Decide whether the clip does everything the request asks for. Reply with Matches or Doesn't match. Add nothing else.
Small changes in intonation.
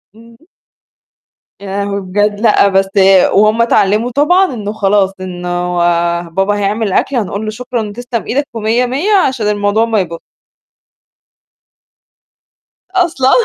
Doesn't match